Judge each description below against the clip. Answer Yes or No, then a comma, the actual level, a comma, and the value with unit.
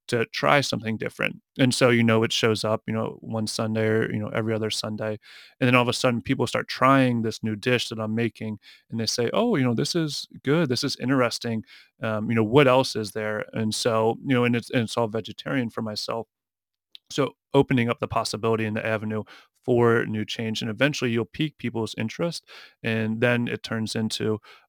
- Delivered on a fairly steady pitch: Yes, narrow, 2.2 semitones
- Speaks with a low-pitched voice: Yes, low, 115 Hz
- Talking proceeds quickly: Yes, fast, 215 wpm